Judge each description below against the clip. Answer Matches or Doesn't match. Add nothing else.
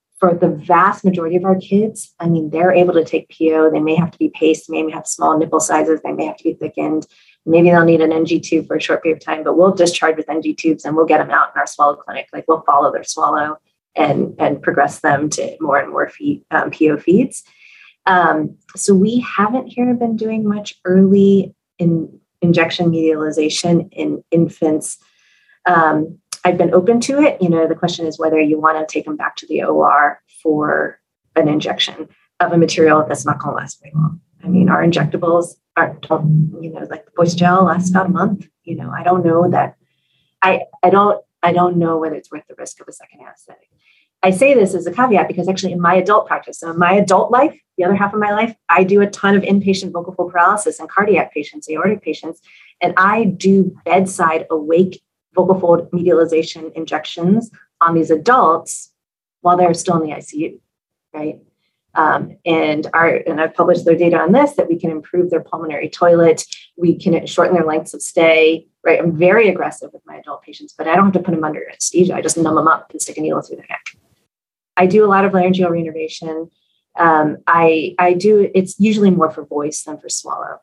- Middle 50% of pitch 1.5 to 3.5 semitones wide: Matches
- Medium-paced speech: Doesn't match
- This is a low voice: Doesn't match